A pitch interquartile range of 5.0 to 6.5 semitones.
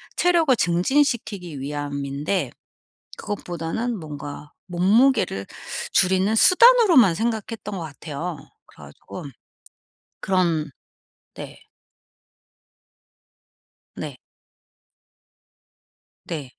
No: wide, 7.1 semitones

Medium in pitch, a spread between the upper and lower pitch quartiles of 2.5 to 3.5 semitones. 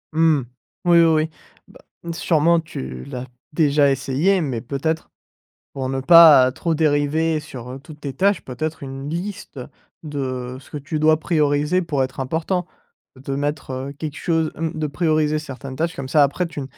Yes: medium, 150 Hz; average, 3.2 semitones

